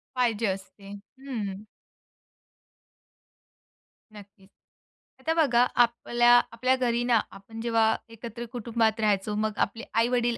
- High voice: Yes, high, 230 Hz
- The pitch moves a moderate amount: No, narrow, 2.2 semitones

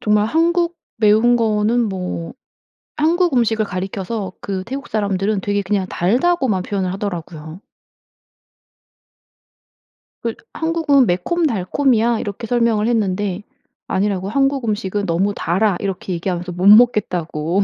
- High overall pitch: Yes, high, 210 Hz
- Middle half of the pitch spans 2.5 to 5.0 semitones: Yes, average, 4.3 semitones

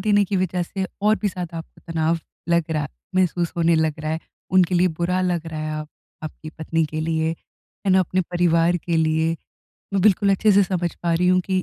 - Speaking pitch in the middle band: Yes, medium, 170 Hz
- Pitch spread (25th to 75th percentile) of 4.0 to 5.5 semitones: No, narrow, 2.4 semitones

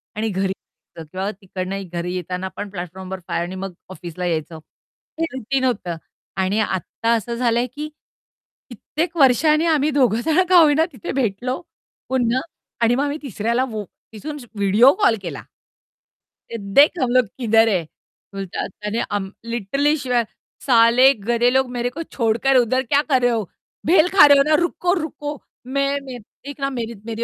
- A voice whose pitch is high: Yes, high, 240 Hz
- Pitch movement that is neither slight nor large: No, wide, 5.8 semitones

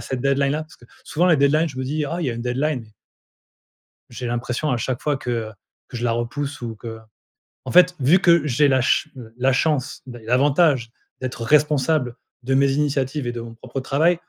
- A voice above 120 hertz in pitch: Yes, low, 135 Hz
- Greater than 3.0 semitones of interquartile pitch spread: Yes, average, 3.7 semitones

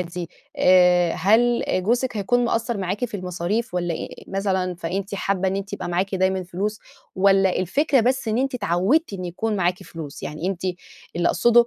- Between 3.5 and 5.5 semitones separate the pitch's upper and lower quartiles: Yes, average, 3.9 semitones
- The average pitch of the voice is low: No, high, 190 Hz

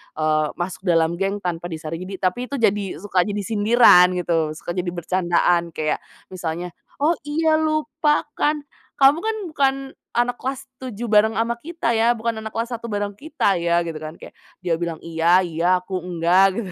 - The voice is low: No, high, 195 Hz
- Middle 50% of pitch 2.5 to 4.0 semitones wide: No, wide, 5.6 semitones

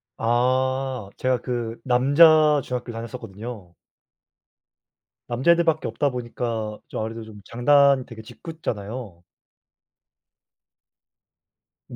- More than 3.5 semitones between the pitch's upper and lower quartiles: No, average, 3.2 semitones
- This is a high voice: No, low, 125 Hz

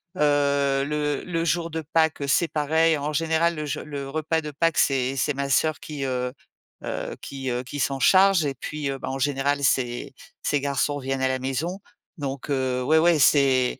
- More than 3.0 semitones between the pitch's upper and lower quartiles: No, average, 2.7 semitones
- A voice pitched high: No, medium, 145 Hz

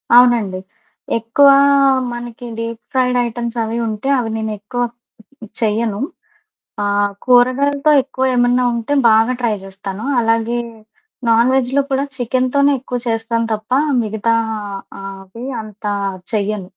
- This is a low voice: No, high, 230 Hz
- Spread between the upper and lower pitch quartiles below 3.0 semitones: Yes, narrow, 2.4 semitones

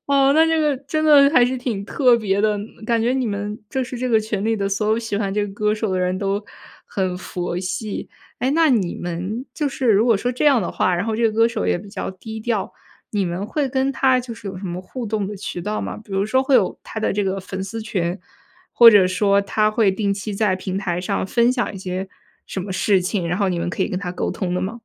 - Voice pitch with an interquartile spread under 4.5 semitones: Yes, average, 3.9 semitones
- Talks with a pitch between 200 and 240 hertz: Yes, high, 210 Hz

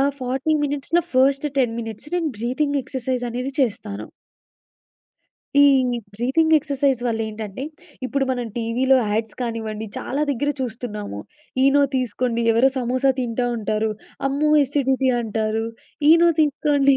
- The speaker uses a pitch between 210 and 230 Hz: No, very high, 255 Hz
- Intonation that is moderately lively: Yes, average, 3.5 semitones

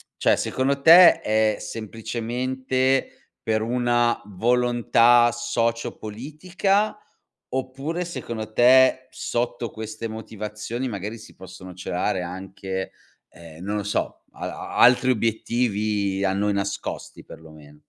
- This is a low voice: Yes, low, 115 Hz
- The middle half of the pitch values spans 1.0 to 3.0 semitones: No, average, 3.6 semitones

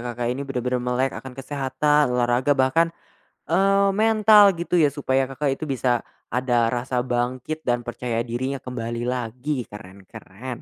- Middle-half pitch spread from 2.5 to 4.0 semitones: Yes, average, 3.1 semitones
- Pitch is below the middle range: Yes, low, 130 Hz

